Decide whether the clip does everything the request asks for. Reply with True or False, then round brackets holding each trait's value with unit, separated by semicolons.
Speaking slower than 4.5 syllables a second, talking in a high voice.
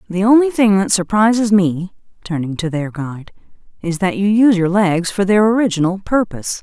False (5.5 syllables/s; 195 Hz)